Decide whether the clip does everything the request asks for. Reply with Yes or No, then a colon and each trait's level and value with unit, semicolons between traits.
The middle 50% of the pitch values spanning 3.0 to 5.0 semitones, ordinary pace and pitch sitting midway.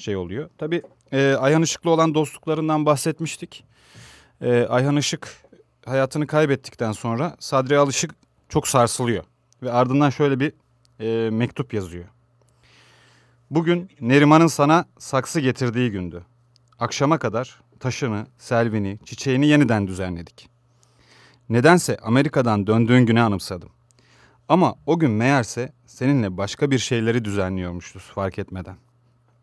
No: average, 3.9 semitones; average, 110 wpm; low, 125 Hz